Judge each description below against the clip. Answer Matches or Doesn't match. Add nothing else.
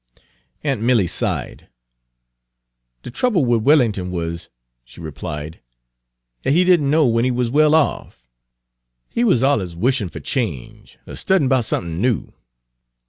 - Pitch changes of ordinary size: Doesn't match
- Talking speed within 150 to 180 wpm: Doesn't match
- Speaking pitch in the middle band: Doesn't match